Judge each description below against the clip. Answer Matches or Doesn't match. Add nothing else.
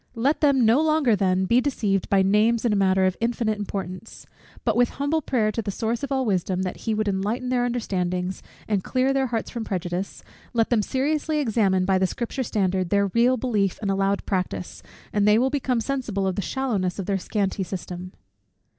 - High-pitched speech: Matches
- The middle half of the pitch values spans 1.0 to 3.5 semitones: Doesn't match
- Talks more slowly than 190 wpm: Doesn't match